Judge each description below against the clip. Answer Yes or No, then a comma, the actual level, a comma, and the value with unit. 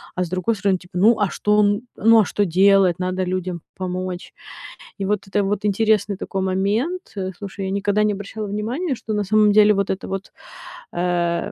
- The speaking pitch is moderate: No, high, 200 Hz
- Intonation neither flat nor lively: No, narrow, 2.2 semitones